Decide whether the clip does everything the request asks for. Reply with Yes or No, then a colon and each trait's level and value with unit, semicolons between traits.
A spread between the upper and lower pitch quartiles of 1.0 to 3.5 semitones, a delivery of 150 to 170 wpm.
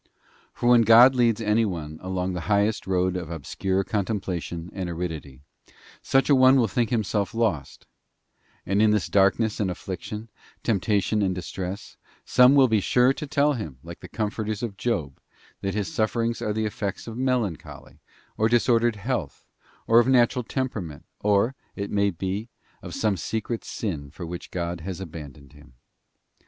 No: average, 4.3 semitones; average, 165 wpm